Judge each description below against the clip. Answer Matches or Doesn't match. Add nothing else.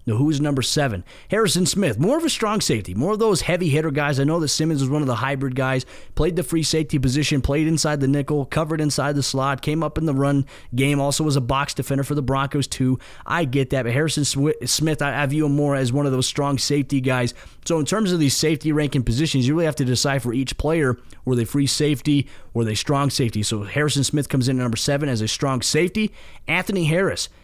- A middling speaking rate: Doesn't match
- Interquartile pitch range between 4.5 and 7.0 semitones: Doesn't match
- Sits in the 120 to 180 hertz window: Matches